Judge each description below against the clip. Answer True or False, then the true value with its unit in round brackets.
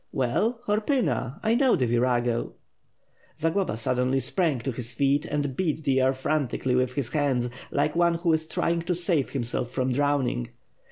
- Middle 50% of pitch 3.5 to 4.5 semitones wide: False (4.9 semitones)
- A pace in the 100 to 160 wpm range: False (170 wpm)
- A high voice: False (140 Hz)